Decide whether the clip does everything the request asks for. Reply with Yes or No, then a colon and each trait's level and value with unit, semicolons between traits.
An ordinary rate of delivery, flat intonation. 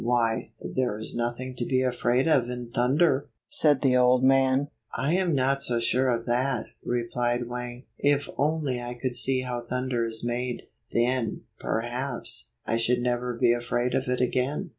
Yes: average, 170 wpm; narrow, 1.5 semitones